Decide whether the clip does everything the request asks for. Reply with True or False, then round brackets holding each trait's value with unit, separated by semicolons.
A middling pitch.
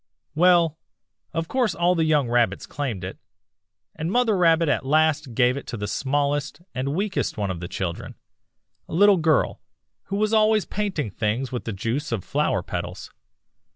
True (150 Hz)